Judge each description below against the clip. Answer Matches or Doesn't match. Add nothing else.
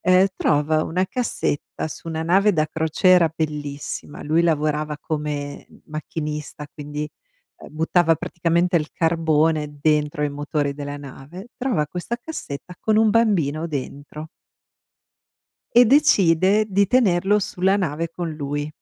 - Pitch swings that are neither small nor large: Matches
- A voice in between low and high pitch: Matches